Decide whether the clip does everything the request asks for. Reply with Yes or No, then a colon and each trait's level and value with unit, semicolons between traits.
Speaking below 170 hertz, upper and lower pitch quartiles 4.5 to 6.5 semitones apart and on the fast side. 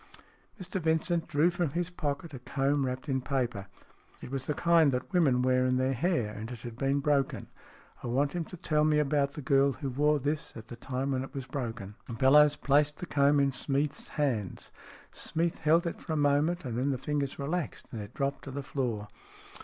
No: medium, 140 Hz; average, 2.9 semitones; fast, 225 wpm